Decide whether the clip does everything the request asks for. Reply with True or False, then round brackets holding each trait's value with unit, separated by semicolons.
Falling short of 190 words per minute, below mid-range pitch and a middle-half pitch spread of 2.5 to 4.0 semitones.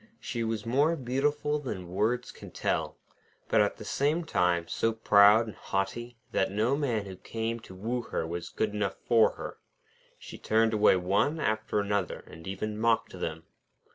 True (170 wpm; 110 Hz; 3.7 semitones)